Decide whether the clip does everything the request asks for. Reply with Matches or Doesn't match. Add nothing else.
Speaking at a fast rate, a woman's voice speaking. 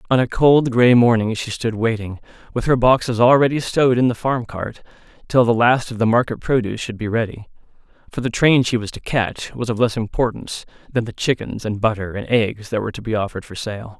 Doesn't match